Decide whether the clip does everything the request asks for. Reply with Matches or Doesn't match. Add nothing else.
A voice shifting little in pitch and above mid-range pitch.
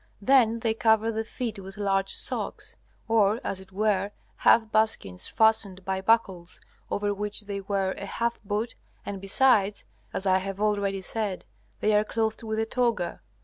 Matches